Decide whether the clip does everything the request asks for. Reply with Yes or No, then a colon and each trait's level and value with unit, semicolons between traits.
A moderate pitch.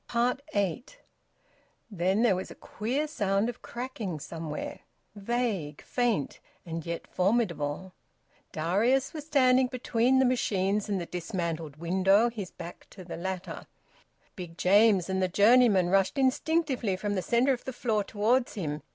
No: high, 205 Hz